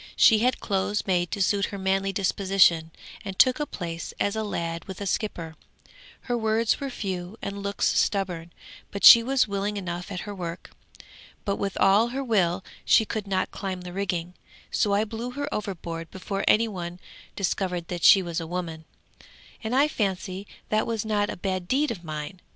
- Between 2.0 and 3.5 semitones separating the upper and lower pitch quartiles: Yes, average, 3.2 semitones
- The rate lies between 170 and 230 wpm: Yes, average, 185 wpm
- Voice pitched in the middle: No, high, 195 Hz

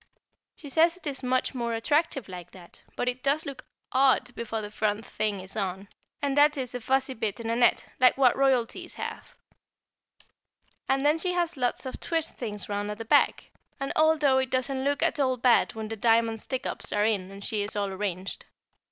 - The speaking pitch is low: No, high, 245 Hz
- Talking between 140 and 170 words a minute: No, fast, 205 wpm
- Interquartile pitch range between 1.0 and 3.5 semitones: No, average, 4.4 semitones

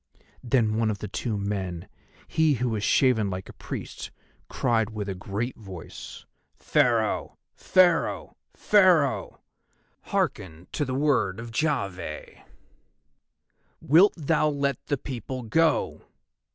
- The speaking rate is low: Yes, slow, 120 wpm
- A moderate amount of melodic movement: No, wide, 6.0 semitones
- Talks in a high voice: No, low, 120 Hz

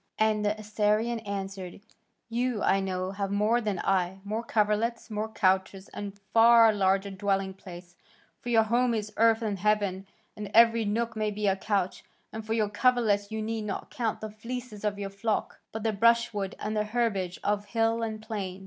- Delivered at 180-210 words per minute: Yes, average, 185 wpm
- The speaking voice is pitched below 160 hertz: No, high, 210 Hz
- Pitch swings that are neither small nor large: No, narrow, 2.3 semitones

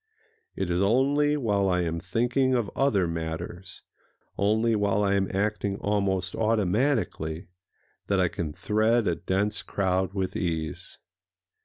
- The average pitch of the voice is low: Yes, low, 100 Hz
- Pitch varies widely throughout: No, average, 3.4 semitones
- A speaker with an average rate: No, slow, 125 wpm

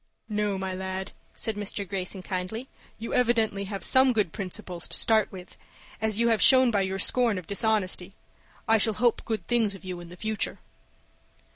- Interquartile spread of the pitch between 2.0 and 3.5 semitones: Yes, average, 2.9 semitones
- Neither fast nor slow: Yes, average, 180 wpm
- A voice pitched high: Yes, high, 205 Hz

